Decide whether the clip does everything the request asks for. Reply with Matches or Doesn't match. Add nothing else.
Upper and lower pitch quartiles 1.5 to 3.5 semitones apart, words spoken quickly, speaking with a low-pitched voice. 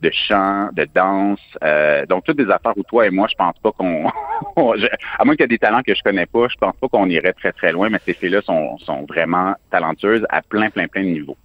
Matches